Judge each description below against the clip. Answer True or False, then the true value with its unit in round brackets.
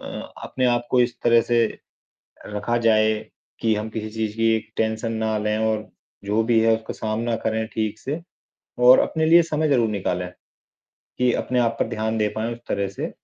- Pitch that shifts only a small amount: True (1.7 semitones)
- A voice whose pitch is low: True (110 Hz)